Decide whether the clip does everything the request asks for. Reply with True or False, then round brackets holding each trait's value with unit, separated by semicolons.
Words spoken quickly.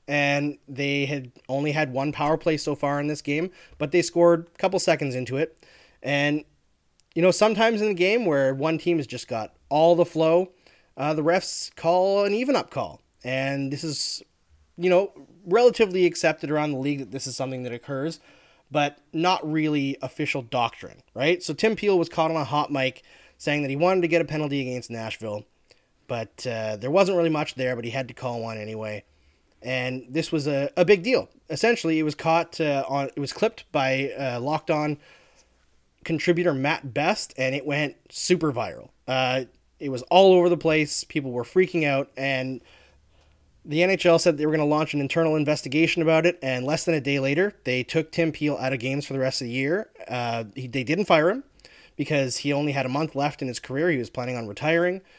True (210 wpm)